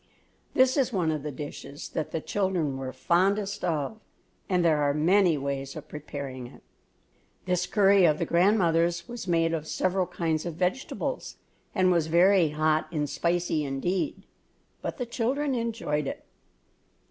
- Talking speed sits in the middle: Yes, average, 155 wpm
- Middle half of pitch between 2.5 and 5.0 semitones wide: Yes, average, 4.3 semitones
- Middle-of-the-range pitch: Yes, medium, 170 Hz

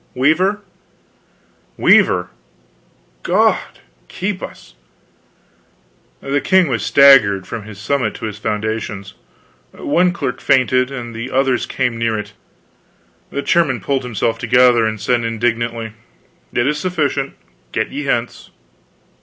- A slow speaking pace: Yes, slow, 120 wpm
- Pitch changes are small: No, average, 3.8 semitones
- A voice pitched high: No, low, 125 Hz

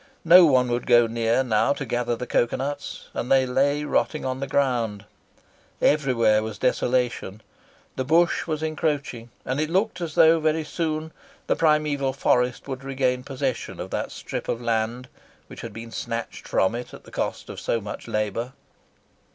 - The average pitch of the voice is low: Yes, low, 130 Hz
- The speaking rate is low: No, average, 175 wpm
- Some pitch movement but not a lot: Yes, average, 4.0 semitones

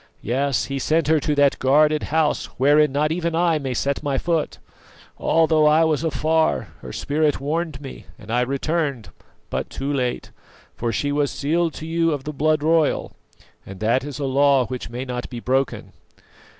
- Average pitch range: Yes, average, 3.0 semitones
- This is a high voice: No, medium, 145 Hz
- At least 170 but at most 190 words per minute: Yes, average, 180 wpm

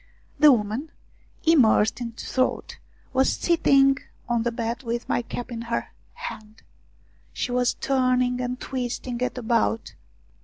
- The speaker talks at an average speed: No, slow, 130 wpm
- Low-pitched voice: No, high, 245 Hz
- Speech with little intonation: Yes, narrow, 2.1 semitones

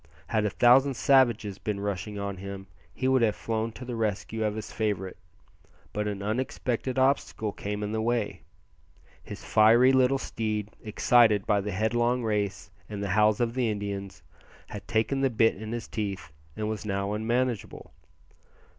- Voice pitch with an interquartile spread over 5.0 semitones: No, narrow, 2.6 semitones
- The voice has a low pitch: Yes, low, 110 Hz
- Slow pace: No, average, 165 wpm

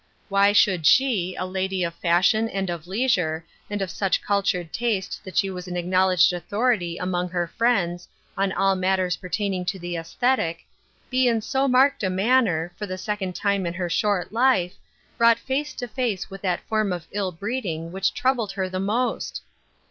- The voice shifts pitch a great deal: No, average, 3.5 semitones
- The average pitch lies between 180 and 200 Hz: Yes, high, 190 Hz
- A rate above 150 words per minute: Yes, average, 180 wpm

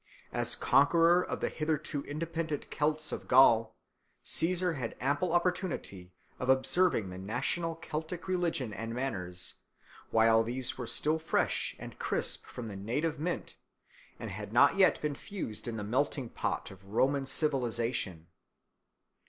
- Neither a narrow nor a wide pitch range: No, wide, 6.2 semitones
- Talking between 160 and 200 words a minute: No, average, 140 wpm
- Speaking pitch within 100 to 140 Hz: Yes, low, 135 Hz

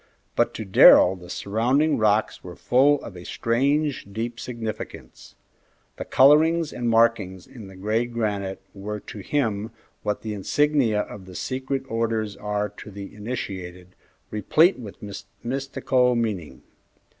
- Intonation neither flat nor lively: Yes, average, 4.1 semitones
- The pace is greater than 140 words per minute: No, slow, 135 wpm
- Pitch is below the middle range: Yes, low, 110 Hz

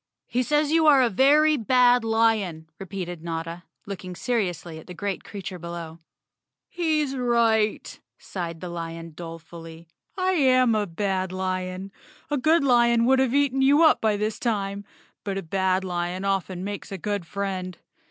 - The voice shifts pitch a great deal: Yes, wide, 5.8 semitones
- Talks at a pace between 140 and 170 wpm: Yes, average, 160 wpm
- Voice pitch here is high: Yes, high, 200 Hz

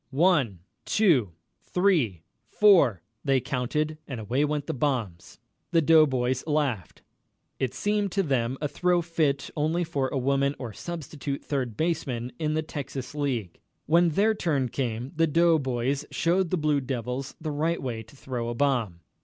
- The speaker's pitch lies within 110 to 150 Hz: Yes, medium, 140 Hz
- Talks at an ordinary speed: Yes, average, 160 wpm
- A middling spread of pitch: Yes, average, 4.5 semitones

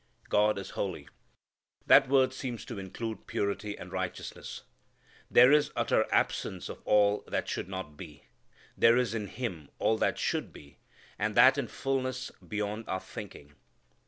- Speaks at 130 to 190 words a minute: Yes, average, 155 wpm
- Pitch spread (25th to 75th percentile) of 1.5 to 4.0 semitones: No, average, 4.5 semitones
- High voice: No, low, 110 Hz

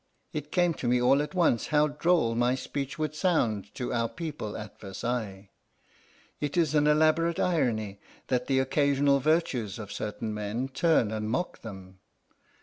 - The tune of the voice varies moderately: No, wide, 5.7 semitones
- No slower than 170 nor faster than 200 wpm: No, average, 160 wpm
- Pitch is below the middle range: Yes, low, 130 Hz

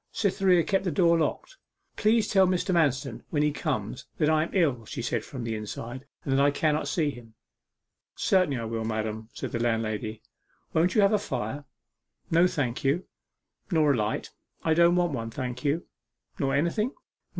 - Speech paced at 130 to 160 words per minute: No, average, 185 wpm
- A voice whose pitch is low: No, medium, 145 Hz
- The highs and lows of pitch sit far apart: Yes, wide, 6.6 semitones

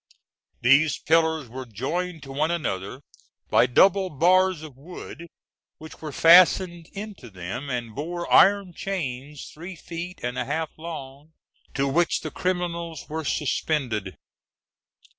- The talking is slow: Yes, slow, 130 wpm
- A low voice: No, medium, 155 Hz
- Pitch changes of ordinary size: Yes, average, 4.6 semitones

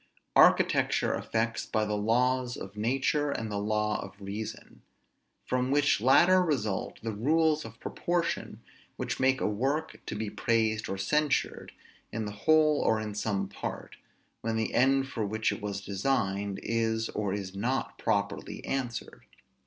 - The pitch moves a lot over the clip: No, average, 4.4 semitones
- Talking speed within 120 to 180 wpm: Yes, average, 155 wpm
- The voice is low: Yes, low, 110 Hz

